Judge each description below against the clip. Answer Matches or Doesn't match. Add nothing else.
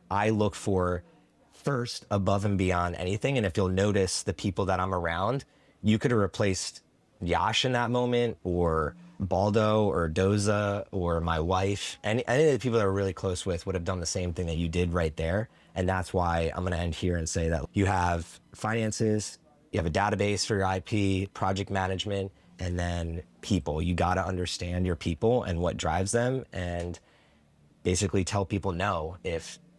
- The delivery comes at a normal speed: Matches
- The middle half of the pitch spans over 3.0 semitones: Doesn't match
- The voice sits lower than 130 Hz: Matches